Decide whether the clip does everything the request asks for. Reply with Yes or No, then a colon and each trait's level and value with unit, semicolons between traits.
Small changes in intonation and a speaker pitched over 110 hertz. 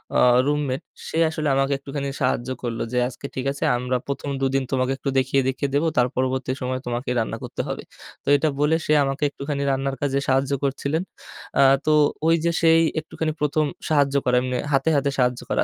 Yes: narrow, 2.1 semitones; low, 135 Hz